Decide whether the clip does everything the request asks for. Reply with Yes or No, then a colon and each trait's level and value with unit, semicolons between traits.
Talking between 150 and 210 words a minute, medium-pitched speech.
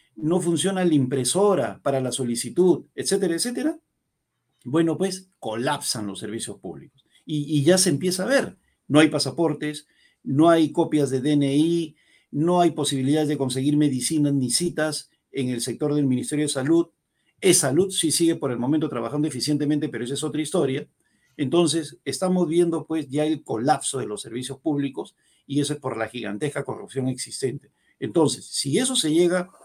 Yes: average, 170 wpm; medium, 150 Hz